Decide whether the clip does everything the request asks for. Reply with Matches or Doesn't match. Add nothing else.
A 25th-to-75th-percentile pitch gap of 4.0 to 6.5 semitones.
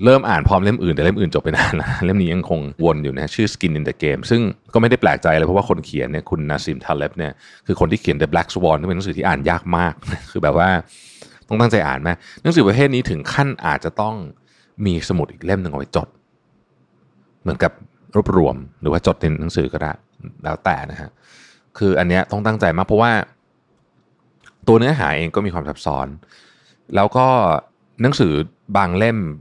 Matches